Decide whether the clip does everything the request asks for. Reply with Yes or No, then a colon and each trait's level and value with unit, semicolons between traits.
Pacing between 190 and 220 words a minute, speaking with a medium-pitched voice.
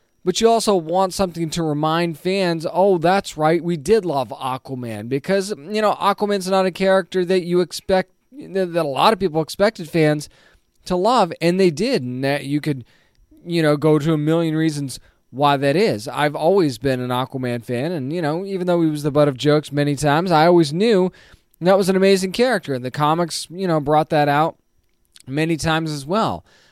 Yes: average, 200 wpm; medium, 165 Hz